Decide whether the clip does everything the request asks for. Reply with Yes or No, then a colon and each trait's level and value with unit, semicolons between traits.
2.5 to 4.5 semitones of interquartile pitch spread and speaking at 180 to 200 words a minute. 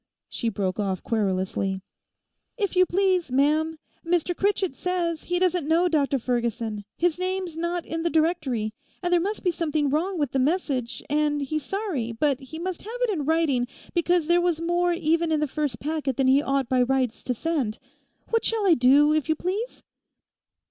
No: average, 5.0 semitones; average, 185 wpm